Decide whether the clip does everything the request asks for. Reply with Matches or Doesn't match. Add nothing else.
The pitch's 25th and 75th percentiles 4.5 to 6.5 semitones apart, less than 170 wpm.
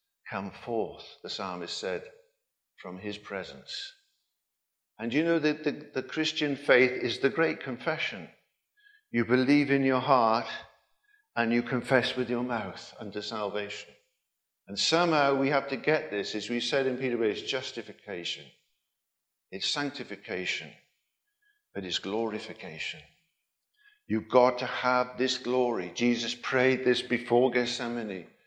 Matches